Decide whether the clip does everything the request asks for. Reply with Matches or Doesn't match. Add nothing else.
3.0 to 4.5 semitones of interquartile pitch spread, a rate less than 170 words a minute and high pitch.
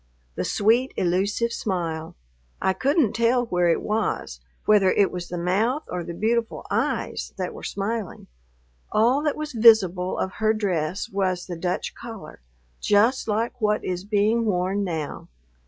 Matches